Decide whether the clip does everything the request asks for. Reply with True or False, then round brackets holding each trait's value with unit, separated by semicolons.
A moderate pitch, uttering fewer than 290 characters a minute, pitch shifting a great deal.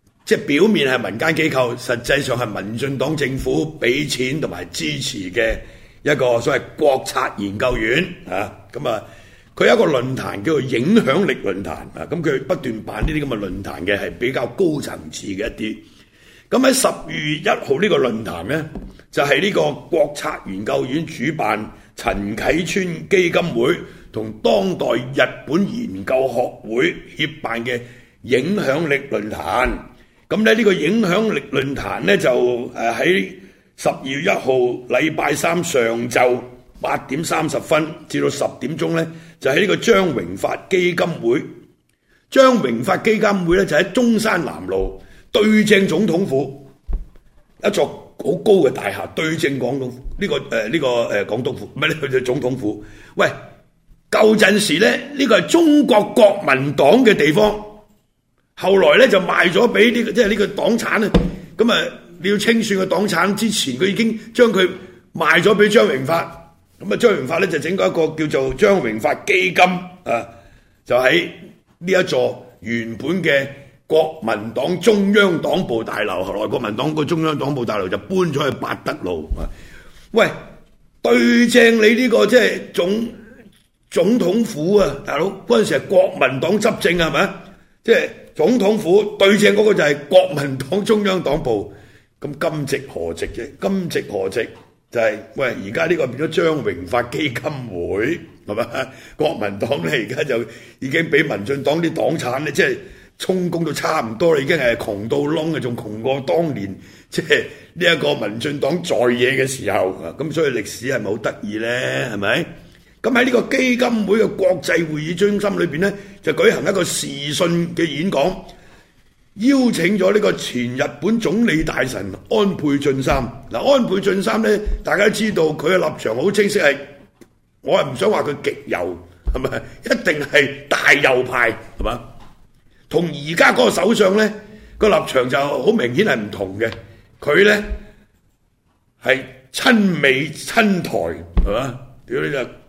True (160 Hz; 240 characters per minute; 8.4 semitones)